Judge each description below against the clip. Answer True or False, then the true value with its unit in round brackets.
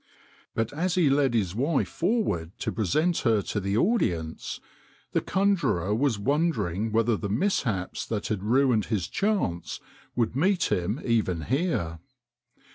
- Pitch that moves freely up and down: True (7.9 semitones)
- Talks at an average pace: True (145 wpm)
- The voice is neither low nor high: False (115 Hz)